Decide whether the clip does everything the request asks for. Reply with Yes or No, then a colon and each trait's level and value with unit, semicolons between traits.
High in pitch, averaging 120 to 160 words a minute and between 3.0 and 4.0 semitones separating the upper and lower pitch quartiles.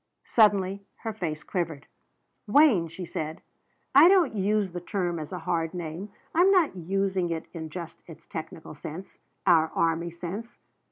No: medium, 180 Hz; average, 155 wpm; average, 3.7 semitones